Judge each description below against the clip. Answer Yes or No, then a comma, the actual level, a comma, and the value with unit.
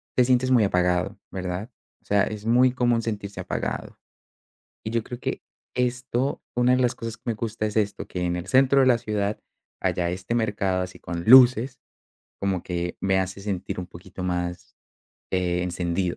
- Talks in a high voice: No, low, 105 Hz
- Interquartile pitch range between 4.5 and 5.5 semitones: Yes, average, 4.9 semitones